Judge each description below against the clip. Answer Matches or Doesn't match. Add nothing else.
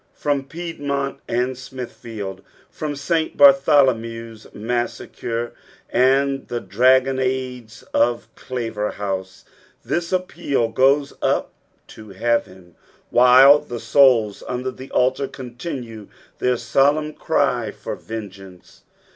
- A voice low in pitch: Matches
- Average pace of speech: Doesn't match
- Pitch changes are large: Doesn't match